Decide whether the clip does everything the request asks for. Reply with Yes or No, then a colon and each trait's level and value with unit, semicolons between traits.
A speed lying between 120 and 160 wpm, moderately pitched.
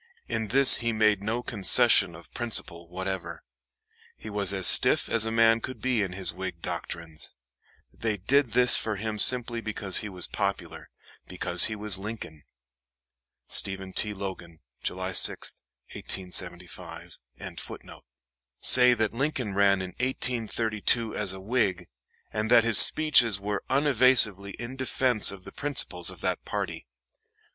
No: average, 140 wpm; low, 105 Hz